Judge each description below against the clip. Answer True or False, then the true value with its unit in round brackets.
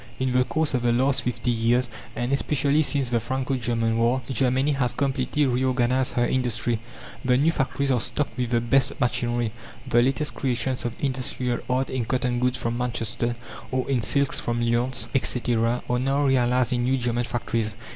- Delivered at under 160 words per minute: False (180 wpm)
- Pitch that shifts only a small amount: True (1.8 semitones)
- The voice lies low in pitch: True (125 Hz)